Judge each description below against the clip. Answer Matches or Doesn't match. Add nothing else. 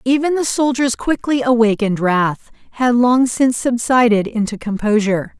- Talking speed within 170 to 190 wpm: Doesn't match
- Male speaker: Doesn't match